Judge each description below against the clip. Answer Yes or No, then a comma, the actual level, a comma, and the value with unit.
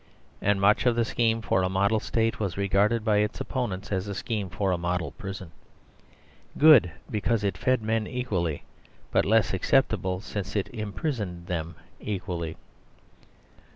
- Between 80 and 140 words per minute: No, average, 155 wpm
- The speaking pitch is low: Yes, low, 100 Hz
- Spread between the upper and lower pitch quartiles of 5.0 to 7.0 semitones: No, average, 3.4 semitones